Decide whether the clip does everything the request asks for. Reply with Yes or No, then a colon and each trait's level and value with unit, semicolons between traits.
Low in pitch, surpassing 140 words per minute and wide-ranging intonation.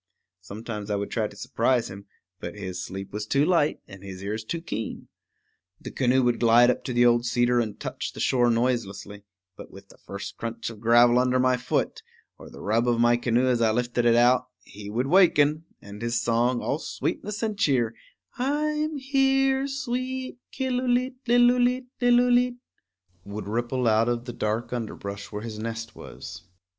Yes: low, 120 Hz; average, 180 wpm; wide, 8.4 semitones